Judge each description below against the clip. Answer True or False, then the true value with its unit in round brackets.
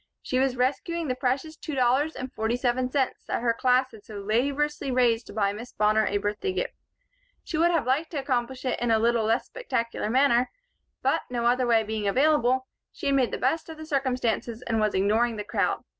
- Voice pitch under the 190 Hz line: False (250 Hz)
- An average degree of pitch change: True (3.2 semitones)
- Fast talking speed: True (210 wpm)